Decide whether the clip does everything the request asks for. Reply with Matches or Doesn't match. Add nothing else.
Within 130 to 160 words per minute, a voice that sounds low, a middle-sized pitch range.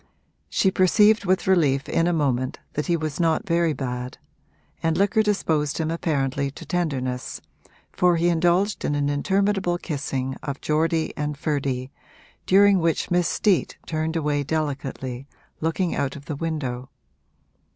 Doesn't match